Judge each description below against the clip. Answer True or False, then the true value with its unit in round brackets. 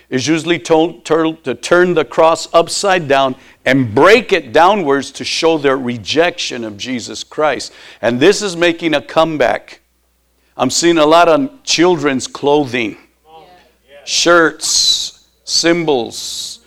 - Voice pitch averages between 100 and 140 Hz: False (160 Hz)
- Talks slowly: True (125 wpm)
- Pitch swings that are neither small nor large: True (4.6 semitones)